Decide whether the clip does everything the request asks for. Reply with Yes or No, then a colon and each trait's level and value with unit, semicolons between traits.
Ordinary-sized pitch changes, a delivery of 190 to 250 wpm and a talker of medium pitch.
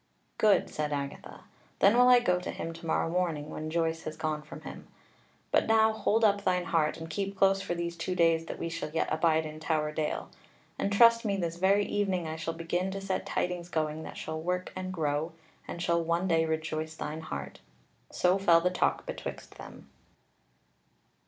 Yes: average, 3.1 semitones; average, 195 wpm; medium, 170 Hz